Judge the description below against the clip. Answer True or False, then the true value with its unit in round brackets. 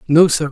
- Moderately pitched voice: True (155 Hz)